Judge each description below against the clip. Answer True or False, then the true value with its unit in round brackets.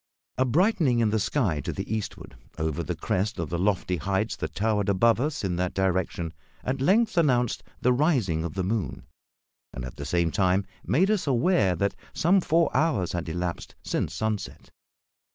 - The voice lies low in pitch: True (105 Hz)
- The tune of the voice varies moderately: False (6.8 semitones)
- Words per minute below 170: False (180 wpm)